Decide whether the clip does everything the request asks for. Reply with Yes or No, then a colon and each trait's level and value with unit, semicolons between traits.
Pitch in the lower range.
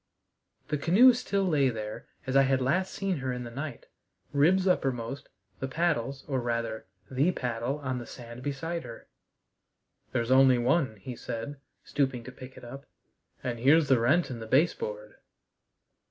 Yes: low, 130 Hz